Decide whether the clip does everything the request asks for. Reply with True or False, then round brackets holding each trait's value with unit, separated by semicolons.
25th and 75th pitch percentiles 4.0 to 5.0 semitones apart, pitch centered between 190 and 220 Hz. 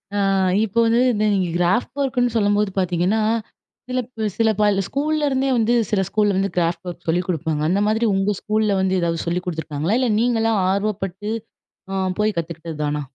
True (4.3 semitones; 205 Hz)